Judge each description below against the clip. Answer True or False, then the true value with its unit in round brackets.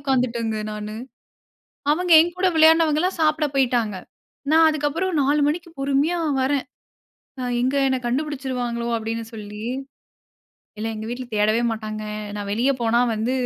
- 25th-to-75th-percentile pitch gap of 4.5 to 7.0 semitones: True (5.3 semitones)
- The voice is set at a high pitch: True (260 Hz)